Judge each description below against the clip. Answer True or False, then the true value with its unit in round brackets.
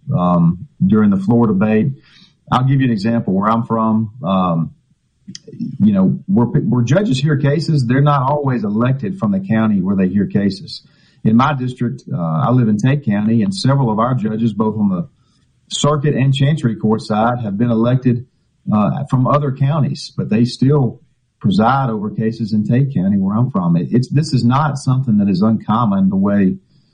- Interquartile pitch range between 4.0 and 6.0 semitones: True (4.7 semitones)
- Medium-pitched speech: False (125 Hz)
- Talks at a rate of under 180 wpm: False (185 wpm)